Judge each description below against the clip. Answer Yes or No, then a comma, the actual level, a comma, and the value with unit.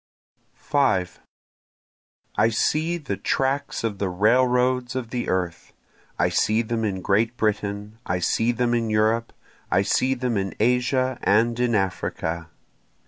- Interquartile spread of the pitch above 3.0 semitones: Yes, average, 3.5 semitones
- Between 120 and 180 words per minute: Yes, average, 140 wpm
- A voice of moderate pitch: No, low, 115 Hz